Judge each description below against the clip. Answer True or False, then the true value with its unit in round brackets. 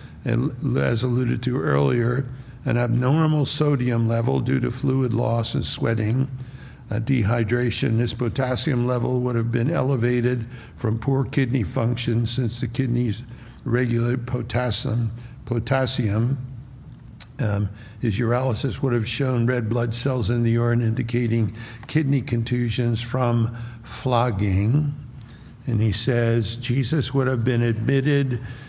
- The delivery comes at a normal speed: False (125 wpm)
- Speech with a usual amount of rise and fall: False (1.9 semitones)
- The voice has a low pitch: True (120 Hz)